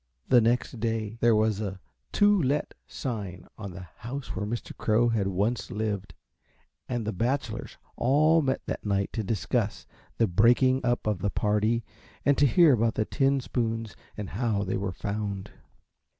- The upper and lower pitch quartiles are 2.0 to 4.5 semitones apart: Yes, average, 3.3 semitones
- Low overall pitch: Yes, low, 110 Hz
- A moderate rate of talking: Yes, average, 165 wpm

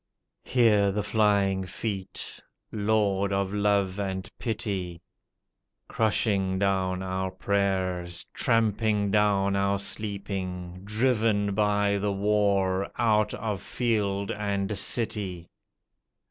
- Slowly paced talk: Yes, slow, 95 wpm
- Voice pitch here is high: No, low, 100 Hz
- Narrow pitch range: Yes, narrow, 1.7 semitones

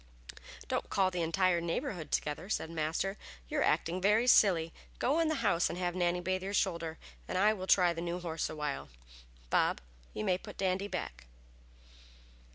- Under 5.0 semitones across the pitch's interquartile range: Yes, average, 2.7 semitones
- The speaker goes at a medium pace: Yes, average, 175 wpm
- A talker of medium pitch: Yes, medium, 180 Hz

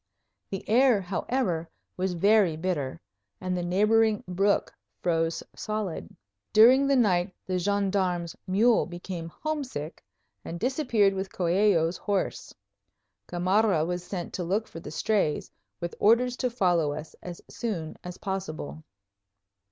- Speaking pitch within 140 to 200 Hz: Yes, medium, 185 Hz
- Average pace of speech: No, slow, 130 wpm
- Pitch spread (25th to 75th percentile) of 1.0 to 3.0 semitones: No, average, 3.8 semitones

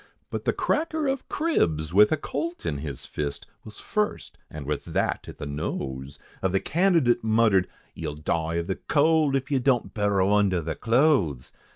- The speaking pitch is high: No, low, 105 Hz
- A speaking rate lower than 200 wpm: Yes, average, 180 wpm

